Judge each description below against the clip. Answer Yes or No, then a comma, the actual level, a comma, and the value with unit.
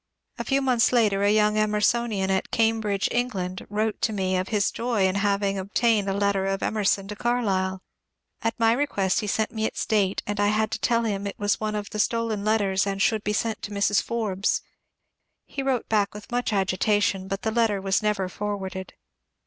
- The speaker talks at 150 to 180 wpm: No, average, 200 wpm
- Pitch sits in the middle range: No, high, 210 Hz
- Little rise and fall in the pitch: Yes, narrow, 2.2 semitones